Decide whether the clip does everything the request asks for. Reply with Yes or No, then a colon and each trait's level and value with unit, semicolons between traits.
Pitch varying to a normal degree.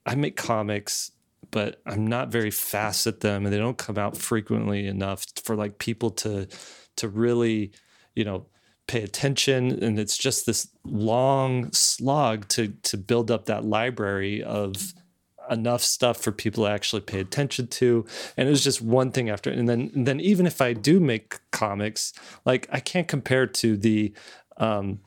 Yes: average, 3.3 semitones